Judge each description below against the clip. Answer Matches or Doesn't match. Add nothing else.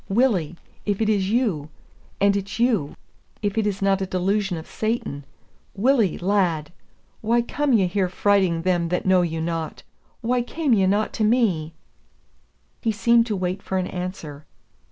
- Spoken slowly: Doesn't match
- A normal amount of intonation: Matches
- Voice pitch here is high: Matches